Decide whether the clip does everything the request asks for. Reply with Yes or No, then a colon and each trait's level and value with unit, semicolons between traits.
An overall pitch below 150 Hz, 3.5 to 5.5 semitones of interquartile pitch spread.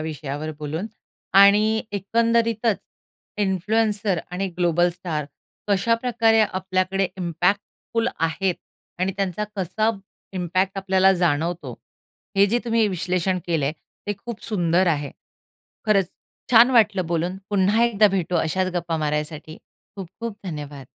No: high, 190 Hz; average, 3.8 semitones